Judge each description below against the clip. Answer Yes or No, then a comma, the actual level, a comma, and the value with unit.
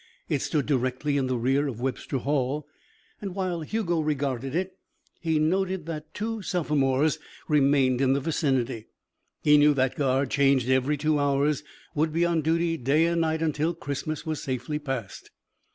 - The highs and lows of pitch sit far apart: No, average, 3.2 semitones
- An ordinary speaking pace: Yes, average, 165 wpm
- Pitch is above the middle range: No, medium, 150 Hz